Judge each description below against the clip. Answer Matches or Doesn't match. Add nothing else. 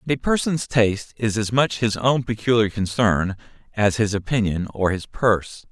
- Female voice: Doesn't match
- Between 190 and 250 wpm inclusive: Doesn't match